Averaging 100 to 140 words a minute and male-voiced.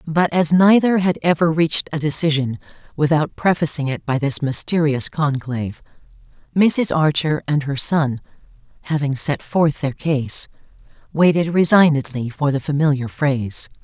No: slow, 135 wpm; female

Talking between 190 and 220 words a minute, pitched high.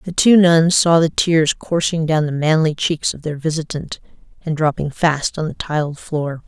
No: average, 195 wpm; medium, 155 Hz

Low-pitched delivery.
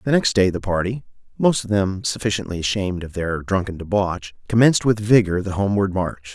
Yes: low, 100 Hz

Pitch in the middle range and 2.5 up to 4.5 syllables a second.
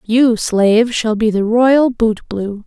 No: high, 225 Hz; 3.5 syllables/s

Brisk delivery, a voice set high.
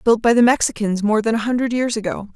Yes: fast, 255 wpm; high, 225 Hz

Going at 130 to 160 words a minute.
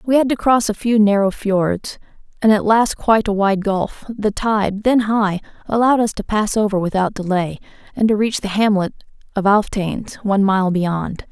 No: average, 190 wpm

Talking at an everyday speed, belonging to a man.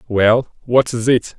Yes: average, 175 wpm; male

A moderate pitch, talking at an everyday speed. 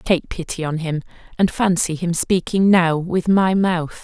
Yes: medium, 175 Hz; average, 180 wpm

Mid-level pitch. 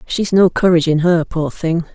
Yes: medium, 170 Hz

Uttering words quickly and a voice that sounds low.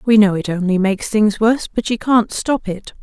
No: fast, 240 wpm; high, 210 Hz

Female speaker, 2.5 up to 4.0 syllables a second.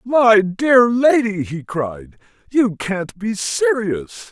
No: male; 2.9 syllables/s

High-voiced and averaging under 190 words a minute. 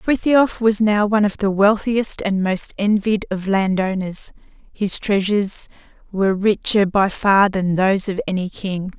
Yes: high, 200 Hz; average, 160 wpm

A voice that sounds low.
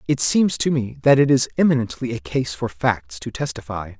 Yes: low, 125 Hz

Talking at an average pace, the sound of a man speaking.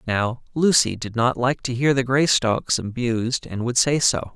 Yes: average, 195 wpm; male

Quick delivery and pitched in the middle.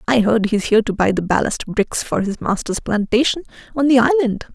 No: fast, 210 wpm; high, 230 Hz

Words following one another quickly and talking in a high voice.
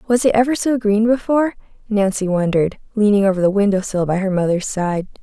No: average, 195 wpm; high, 205 Hz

